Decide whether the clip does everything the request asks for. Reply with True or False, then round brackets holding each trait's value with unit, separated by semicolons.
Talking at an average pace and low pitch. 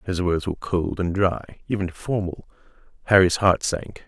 True (160 wpm; 95 Hz)